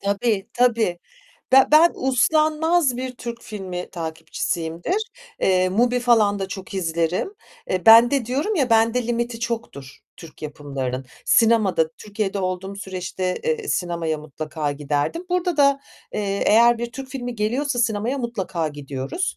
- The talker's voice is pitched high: Yes, high, 220 Hz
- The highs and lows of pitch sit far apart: Yes, wide, 6.0 semitones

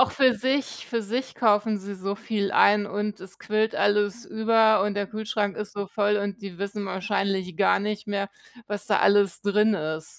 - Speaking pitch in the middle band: No, high, 205 Hz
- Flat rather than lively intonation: Yes, narrow, 1.5 semitones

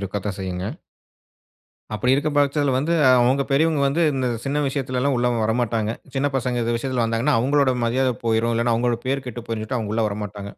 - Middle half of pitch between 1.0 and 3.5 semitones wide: Yes, average, 3.2 semitones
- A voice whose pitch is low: Yes, low, 125 Hz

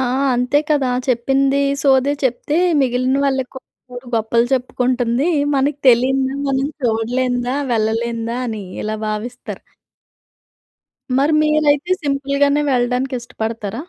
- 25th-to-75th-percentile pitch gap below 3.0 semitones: Yes, narrow, 2.6 semitones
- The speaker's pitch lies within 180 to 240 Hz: No, very high, 255 Hz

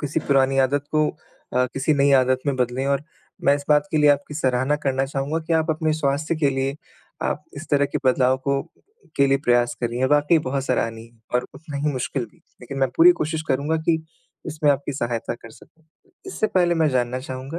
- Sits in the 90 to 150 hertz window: Yes, medium, 140 Hz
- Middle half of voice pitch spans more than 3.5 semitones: No, narrow, 2.5 semitones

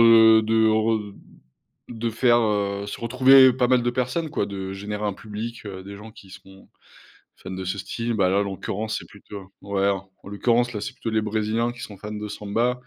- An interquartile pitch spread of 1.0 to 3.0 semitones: Yes, average, 2.7 semitones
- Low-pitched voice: Yes, low, 110 Hz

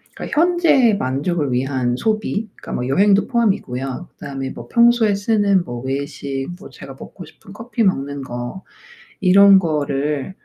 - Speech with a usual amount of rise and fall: No, wide, 7.6 semitones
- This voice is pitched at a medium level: Yes, medium, 175 Hz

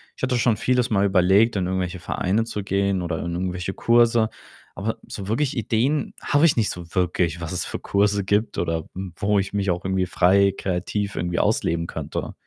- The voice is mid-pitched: No, low, 100 Hz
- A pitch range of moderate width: Yes, average, 3.5 semitones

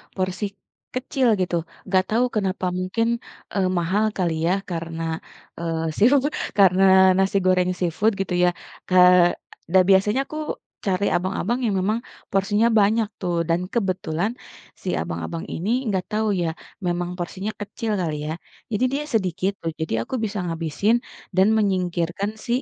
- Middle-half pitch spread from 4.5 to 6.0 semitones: No, average, 3.3 semitones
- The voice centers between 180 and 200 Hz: Yes, high, 190 Hz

